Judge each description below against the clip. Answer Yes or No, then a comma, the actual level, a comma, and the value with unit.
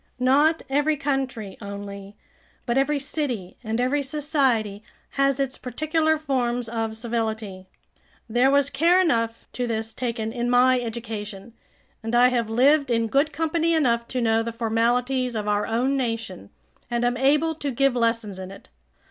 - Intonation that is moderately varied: Yes, average, 3.6 semitones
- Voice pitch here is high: Yes, high, 245 Hz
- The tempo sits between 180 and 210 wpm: No, average, 155 wpm